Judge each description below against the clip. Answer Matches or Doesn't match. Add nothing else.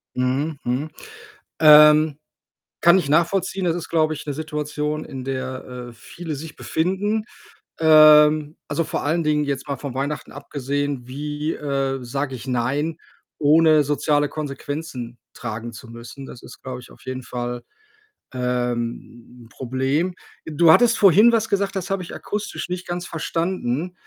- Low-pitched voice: Doesn't match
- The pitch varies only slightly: Doesn't match